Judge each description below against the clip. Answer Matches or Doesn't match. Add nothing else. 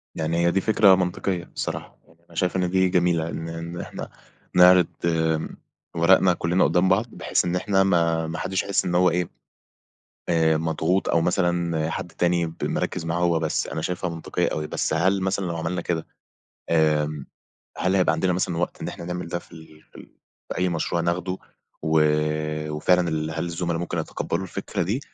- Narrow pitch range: Matches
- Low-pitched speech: Matches